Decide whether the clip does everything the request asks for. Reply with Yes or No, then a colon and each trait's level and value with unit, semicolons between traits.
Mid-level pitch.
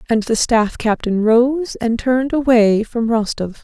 No: high, 235 Hz